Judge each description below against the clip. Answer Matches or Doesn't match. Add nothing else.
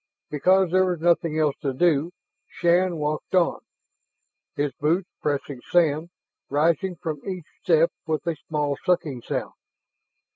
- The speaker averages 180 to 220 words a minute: Doesn't match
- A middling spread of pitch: Matches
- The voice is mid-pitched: Matches